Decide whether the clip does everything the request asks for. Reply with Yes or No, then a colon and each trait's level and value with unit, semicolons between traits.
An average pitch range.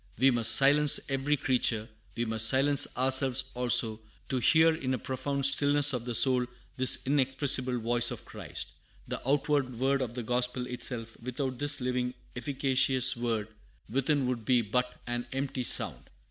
No: narrow, 2.1 semitones